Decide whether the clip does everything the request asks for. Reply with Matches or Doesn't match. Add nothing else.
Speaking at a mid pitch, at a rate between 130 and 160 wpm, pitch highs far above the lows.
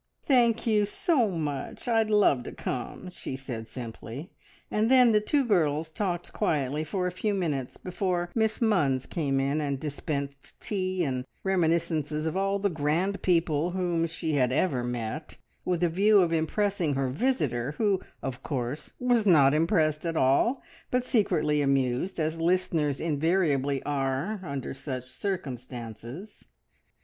Matches